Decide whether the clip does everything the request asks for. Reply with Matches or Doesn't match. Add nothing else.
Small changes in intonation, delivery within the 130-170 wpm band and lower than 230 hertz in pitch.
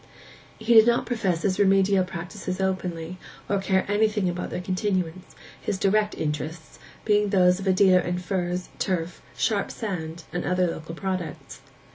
Matches